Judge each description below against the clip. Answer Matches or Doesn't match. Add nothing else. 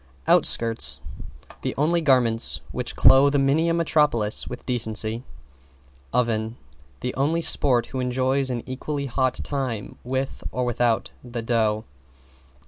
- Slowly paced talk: Matches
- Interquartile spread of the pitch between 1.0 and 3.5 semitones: Matches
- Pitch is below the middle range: Matches